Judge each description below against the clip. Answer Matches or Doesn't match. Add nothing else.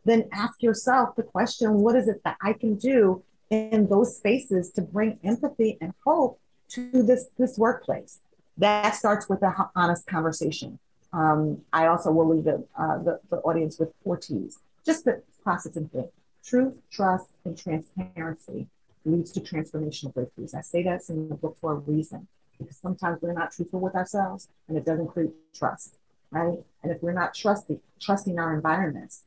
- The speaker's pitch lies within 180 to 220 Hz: Matches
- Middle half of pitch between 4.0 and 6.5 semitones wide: Matches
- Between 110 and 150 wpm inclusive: Doesn't match